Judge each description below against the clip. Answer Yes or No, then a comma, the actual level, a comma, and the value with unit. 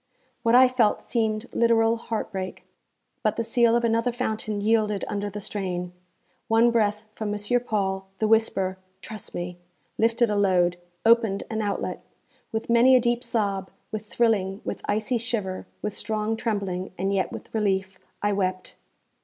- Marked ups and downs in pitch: No, average, 2.8 semitones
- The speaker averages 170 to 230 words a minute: No, average, 155 wpm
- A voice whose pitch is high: Yes, high, 215 Hz